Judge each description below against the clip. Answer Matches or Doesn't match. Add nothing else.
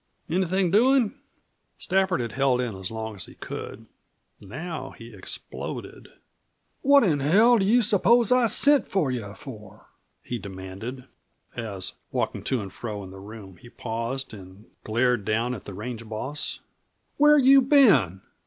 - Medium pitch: Doesn't match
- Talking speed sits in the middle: Matches